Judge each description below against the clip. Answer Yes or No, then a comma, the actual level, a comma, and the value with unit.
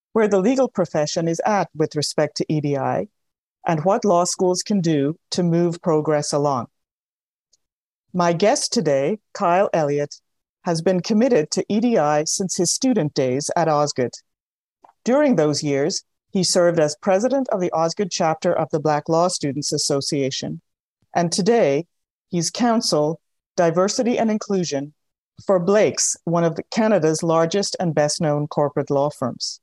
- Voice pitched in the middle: Yes, medium, 170 Hz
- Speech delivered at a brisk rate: No, average, 145 wpm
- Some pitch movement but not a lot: Yes, average, 4.7 semitones